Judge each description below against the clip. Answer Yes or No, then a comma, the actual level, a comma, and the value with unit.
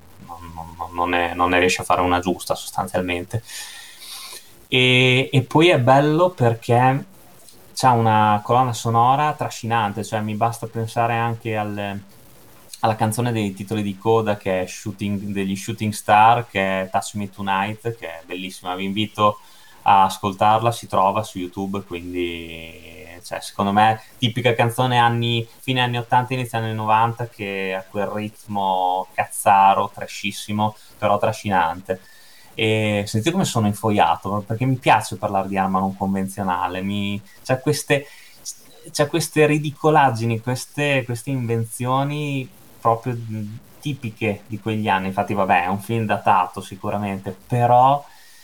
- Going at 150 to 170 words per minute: No, average, 135 wpm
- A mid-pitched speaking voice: No, low, 110 Hz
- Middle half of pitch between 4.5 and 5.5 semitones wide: No, average, 3.5 semitones